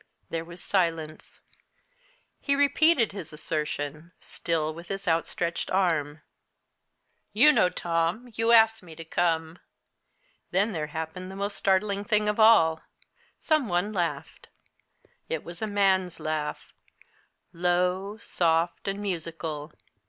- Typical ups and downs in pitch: Yes, average, 3.9 semitones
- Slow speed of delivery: Yes, slow, 125 wpm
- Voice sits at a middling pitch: Yes, medium, 175 Hz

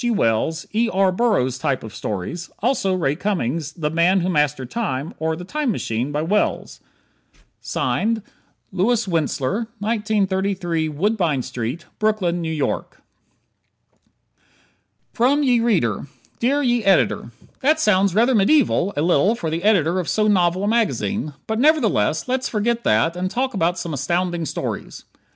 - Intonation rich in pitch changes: Yes, wide, 5.7 semitones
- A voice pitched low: No, medium, 185 Hz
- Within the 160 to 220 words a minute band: No, average, 145 wpm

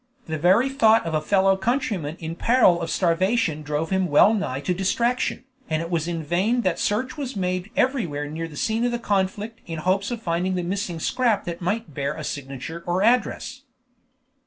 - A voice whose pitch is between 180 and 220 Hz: Yes, medium, 185 Hz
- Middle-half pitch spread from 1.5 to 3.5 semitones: No, average, 5.3 semitones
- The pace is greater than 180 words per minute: Yes, average, 190 wpm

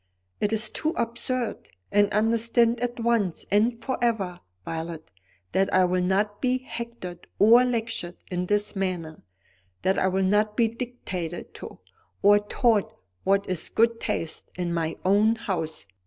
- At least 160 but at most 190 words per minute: No, average, 150 wpm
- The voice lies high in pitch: Yes, high, 205 Hz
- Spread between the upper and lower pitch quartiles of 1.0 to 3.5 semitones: No, average, 4.1 semitones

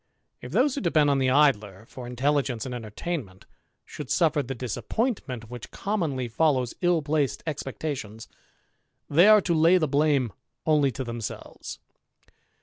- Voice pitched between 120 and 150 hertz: Yes, medium, 140 Hz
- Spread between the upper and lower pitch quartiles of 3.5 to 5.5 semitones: Yes, average, 4.6 semitones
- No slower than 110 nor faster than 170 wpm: Yes, average, 145 wpm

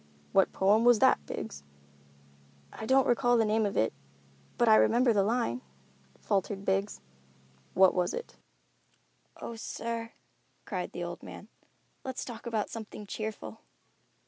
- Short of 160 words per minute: Yes, average, 140 wpm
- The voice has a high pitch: Yes, high, 220 Hz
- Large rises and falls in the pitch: No, average, 3.1 semitones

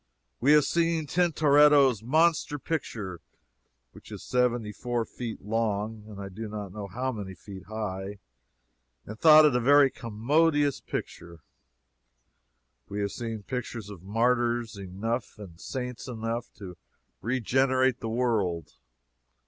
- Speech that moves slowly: Yes, slow, 130 wpm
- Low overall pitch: Yes, low, 115 Hz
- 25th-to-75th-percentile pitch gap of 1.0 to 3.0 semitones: No, average, 4.2 semitones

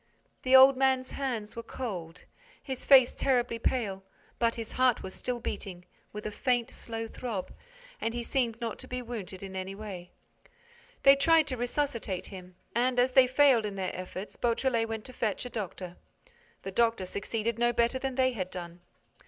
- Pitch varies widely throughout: No, average, 4.4 semitones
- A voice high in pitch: Yes, high, 230 Hz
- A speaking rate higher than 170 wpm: Yes, average, 180 wpm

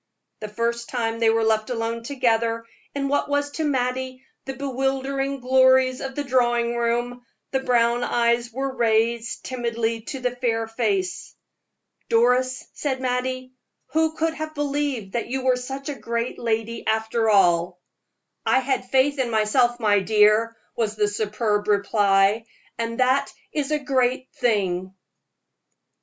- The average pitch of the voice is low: No, high, 240 Hz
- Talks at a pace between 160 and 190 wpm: No, average, 145 wpm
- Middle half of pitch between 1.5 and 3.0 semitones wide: Yes, average, 2.7 semitones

